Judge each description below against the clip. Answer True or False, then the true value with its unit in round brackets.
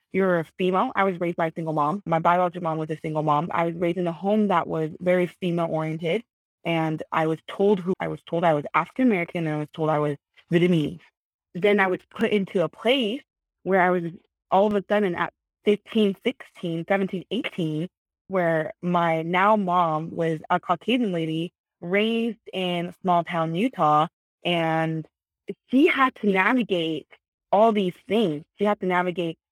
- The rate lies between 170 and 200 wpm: True (185 wpm)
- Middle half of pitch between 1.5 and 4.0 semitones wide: True (3.5 semitones)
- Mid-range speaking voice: True (180 Hz)